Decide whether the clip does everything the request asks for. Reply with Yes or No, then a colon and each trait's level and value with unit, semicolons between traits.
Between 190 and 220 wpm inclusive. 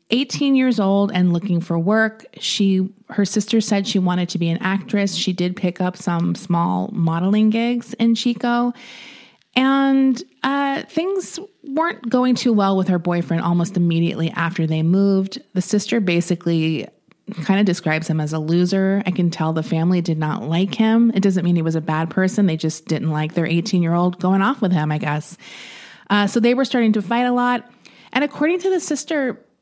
Yes: average, 195 wpm